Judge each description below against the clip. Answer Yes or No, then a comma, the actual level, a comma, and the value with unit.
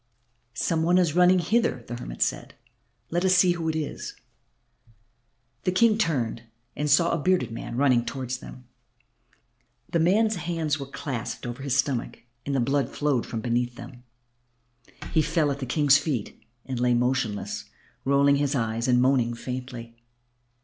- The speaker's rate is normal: Yes, average, 160 wpm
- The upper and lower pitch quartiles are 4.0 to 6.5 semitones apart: Yes, average, 5.1 semitones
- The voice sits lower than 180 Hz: Yes, medium, 140 Hz